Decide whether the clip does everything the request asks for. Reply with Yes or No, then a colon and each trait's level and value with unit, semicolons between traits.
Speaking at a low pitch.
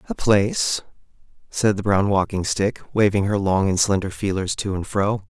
Yes: low, 100 Hz